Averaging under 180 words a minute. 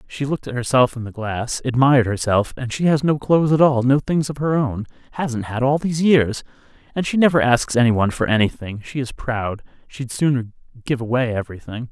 No: fast, 205 wpm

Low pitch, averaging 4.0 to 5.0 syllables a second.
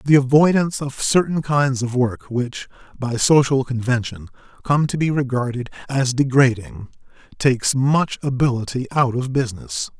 Yes: low, 130 Hz; 4.8 syllables/s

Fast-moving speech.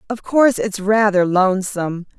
No: slow, 135 wpm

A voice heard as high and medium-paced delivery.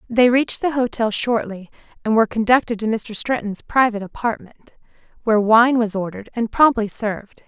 Yes: high, 225 Hz; average, 160 wpm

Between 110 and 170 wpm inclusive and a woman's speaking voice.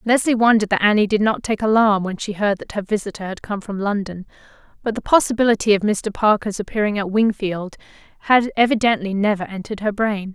No: average, 190 wpm; female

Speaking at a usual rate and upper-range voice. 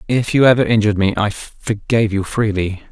No: average, 185 wpm; low, 105 Hz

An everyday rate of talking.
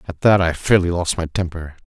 No: fast, 225 wpm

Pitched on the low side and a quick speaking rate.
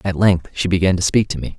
Yes: very low, 95 Hz; fast, 305 wpm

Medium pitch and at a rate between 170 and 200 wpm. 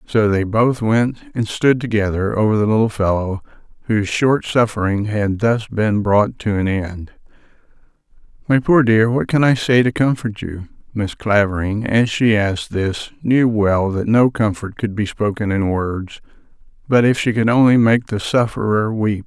No: low, 110 Hz; average, 175 wpm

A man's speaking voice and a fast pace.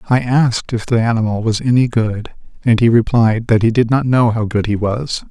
Yes: male; fast, 225 wpm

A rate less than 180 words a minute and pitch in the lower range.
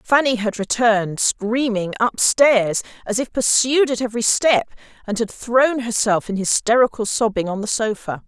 No: average, 160 wpm; high, 225 Hz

